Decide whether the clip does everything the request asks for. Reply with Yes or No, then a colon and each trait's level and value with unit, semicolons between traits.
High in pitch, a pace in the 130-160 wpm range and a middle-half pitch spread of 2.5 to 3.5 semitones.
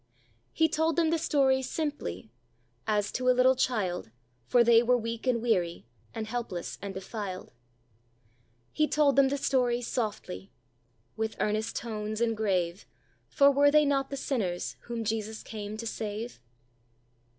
No: high, 230 Hz; average, 150 wpm; average, 4.1 semitones